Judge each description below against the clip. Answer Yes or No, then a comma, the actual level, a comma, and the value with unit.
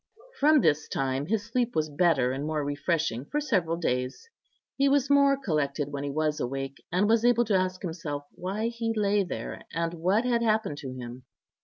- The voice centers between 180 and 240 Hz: No, medium, 170 Hz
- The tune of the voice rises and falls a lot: Yes, wide, 7.8 semitones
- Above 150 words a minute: Yes, average, 190 wpm